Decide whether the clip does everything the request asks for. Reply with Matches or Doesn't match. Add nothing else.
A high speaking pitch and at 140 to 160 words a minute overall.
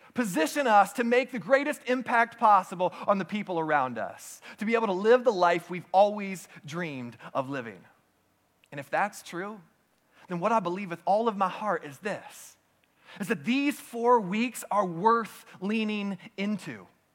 Doesn't match